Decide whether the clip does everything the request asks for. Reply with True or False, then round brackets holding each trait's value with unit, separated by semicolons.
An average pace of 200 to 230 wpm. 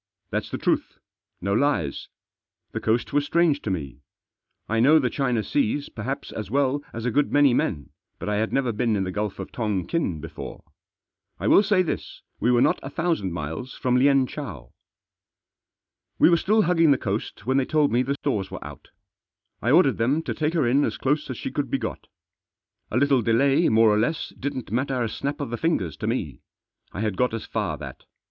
True (205 wpm)